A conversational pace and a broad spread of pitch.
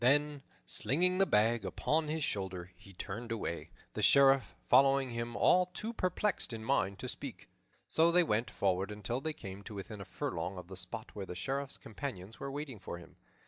Yes: average, 190 wpm; wide, 6.9 semitones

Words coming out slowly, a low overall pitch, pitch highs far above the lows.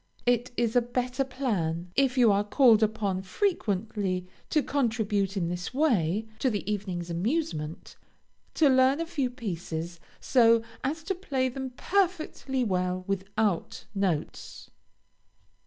No: slow, 130 wpm; high, 225 Hz; wide, 6.0 semitones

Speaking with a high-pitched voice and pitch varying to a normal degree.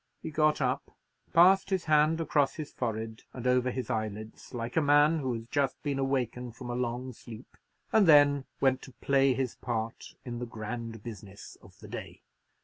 No: low, 130 Hz; average, 3.7 semitones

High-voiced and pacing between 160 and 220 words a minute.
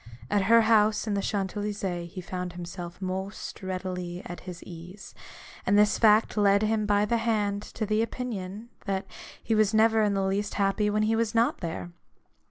Yes: high, 205 Hz; average, 190 wpm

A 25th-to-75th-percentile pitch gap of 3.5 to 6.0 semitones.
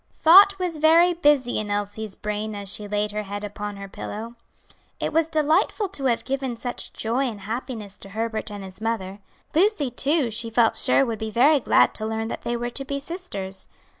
Yes: wide, 5.6 semitones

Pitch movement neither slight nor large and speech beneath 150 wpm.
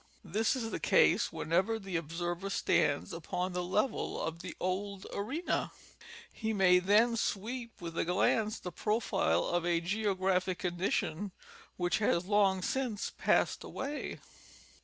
Yes: average, 3.4 semitones; average, 140 wpm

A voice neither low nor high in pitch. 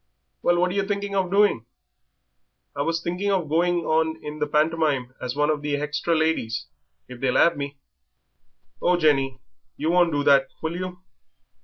Yes: medium, 160 Hz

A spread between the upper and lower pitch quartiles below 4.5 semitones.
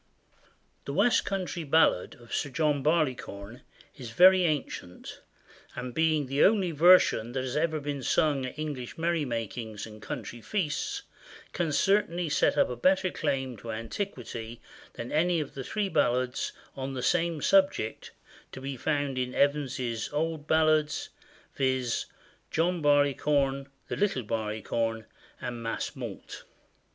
No: average, 4.8 semitones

